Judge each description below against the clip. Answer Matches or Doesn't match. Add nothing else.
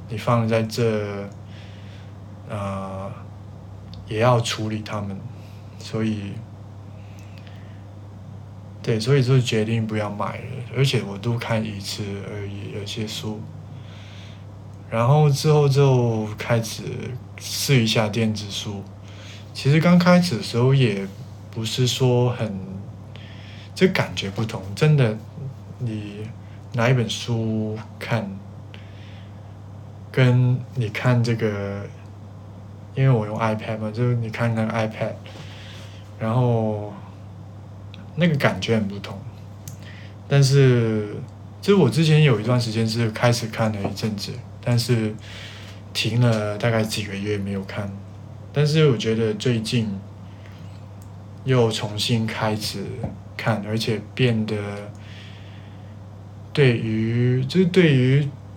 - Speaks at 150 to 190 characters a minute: Matches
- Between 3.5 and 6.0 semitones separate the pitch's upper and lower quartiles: Doesn't match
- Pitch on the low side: Matches